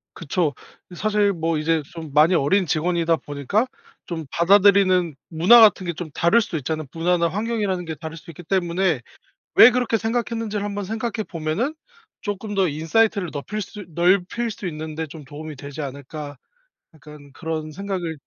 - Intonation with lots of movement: No, average, 4.5 semitones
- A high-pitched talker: No, medium, 175 Hz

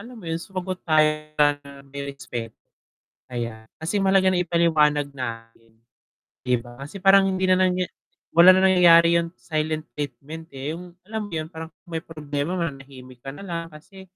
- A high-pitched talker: No, medium, 160 Hz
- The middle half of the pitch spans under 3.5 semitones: No, average, 4.5 semitones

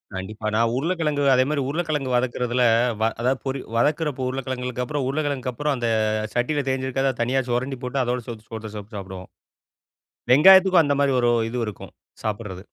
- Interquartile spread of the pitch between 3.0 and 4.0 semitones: Yes, average, 3.4 semitones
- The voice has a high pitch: No, low, 130 Hz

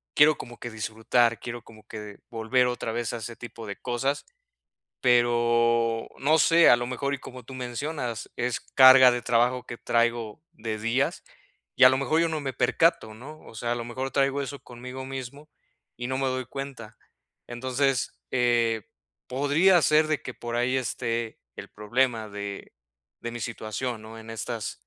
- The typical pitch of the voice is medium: No, low, 120 Hz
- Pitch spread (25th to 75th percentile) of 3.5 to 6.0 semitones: No, narrow, 2.4 semitones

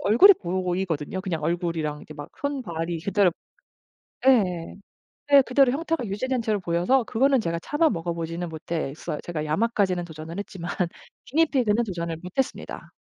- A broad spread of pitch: Yes, wide, 6.6 semitones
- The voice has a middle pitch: Yes, medium, 180 Hz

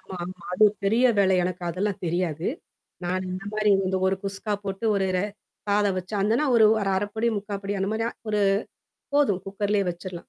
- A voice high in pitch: Yes, high, 195 Hz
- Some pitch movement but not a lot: No, narrow, 2.1 semitones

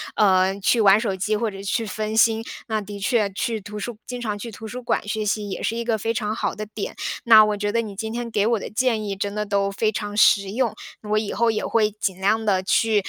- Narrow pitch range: Yes, narrow, 1.8 semitones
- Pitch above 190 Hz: Yes, high, 215 Hz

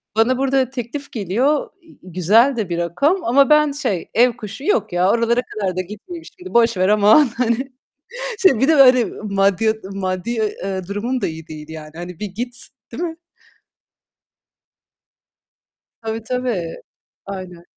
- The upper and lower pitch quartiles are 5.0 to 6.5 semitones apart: Yes, wide, 5.6 semitones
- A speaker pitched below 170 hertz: No, high, 225 Hz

